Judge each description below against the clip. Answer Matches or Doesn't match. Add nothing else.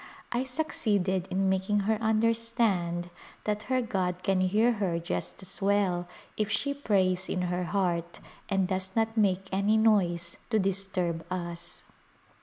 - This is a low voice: Doesn't match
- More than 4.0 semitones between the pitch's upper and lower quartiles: Doesn't match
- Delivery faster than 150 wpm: Doesn't match